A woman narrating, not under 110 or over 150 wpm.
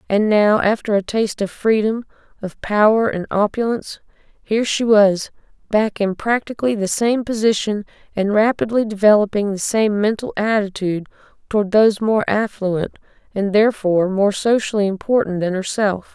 Yes: female; average, 140 wpm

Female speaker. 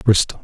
No: male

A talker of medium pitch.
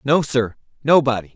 No: low, 130 Hz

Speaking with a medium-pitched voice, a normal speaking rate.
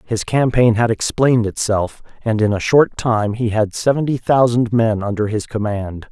No: low, 115 Hz; average, 175 wpm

